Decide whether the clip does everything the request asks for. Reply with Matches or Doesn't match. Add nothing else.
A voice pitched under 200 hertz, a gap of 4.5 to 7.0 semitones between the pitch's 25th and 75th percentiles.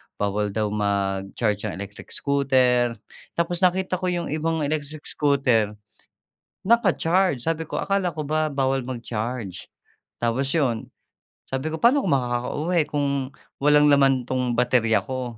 Matches